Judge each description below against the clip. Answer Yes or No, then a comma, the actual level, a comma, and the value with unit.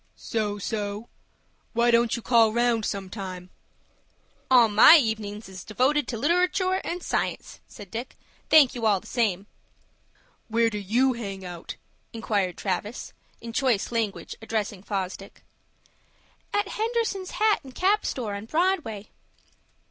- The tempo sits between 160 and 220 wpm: No, slow, 135 wpm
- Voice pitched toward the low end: No, high, 225 Hz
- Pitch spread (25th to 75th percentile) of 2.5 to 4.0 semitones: No, average, 4.5 semitones